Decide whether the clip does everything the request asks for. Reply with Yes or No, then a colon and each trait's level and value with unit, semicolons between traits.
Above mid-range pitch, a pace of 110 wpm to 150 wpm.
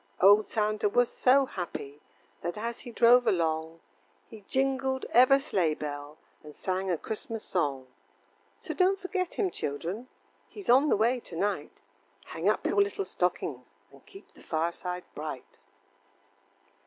Yes: high, 210 Hz; average, 145 wpm